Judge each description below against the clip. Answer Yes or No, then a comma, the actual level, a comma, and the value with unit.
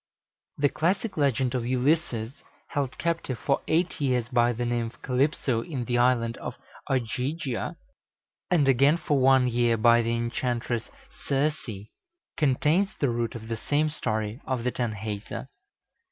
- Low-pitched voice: Yes, low, 125 Hz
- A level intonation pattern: No, average, 3.5 semitones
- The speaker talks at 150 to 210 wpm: No, average, 140 wpm